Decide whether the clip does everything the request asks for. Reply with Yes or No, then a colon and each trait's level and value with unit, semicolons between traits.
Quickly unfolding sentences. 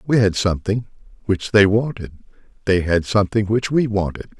No: average, 165 wpm